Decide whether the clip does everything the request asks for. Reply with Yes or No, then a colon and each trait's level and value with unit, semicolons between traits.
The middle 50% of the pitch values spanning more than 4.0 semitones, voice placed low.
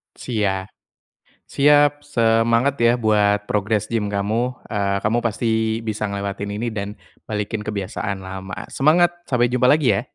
No: average, 3.0 semitones; low, 110 Hz